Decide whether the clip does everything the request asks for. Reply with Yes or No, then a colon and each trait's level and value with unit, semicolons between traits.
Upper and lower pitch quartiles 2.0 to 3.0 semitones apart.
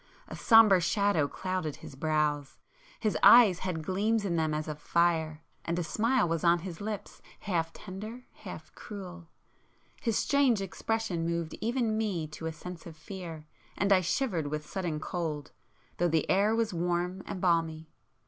No: average, 4.3 semitones